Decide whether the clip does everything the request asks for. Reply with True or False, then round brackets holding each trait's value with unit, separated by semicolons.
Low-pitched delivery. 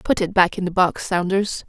False (185 Hz)